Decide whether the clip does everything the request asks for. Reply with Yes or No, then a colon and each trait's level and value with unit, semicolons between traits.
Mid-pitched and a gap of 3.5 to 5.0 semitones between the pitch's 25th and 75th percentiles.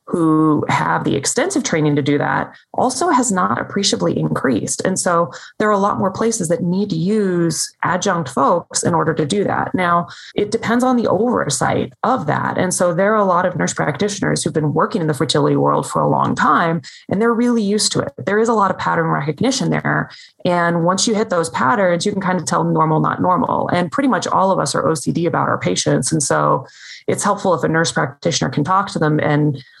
Yes: medium, 180 Hz; average, 4.5 semitones